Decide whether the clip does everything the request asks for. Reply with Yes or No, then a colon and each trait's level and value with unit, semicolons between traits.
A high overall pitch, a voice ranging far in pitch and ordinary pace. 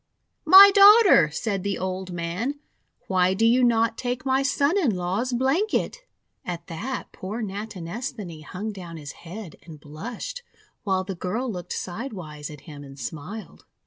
Yes: high, 200 Hz; wide, 6.3 semitones; average, 155 wpm